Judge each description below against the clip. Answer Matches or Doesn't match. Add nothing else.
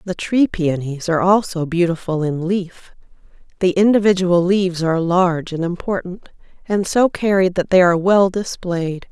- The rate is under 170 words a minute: Matches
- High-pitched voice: Doesn't match